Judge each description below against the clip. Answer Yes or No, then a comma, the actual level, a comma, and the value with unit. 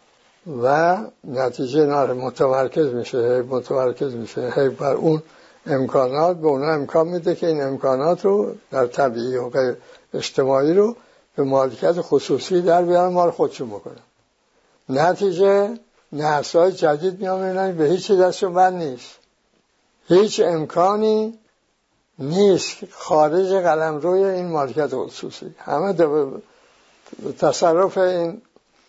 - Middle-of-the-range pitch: Yes, medium, 170 Hz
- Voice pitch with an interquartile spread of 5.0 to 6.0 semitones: Yes, wide, 5.5 semitones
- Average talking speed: No, slow, 110 wpm